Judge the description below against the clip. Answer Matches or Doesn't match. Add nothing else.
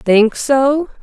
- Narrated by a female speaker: Matches